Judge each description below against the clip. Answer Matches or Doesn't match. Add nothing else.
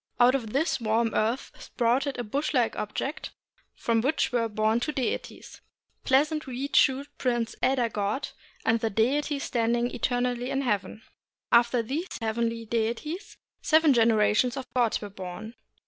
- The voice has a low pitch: Doesn't match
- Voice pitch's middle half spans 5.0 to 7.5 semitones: Doesn't match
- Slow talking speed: Doesn't match